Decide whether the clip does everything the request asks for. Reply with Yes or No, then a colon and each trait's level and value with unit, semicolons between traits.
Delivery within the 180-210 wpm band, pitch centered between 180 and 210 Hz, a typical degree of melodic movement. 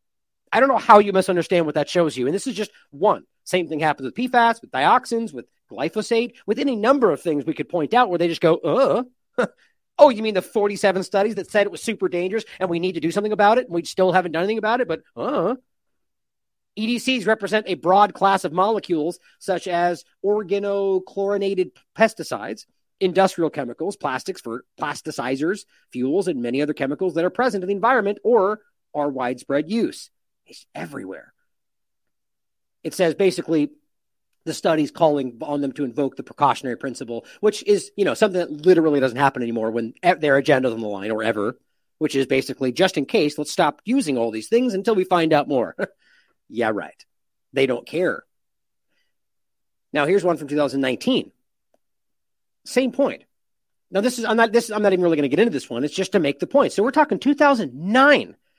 No: average, 190 wpm; medium, 185 Hz; wide, 6.9 semitones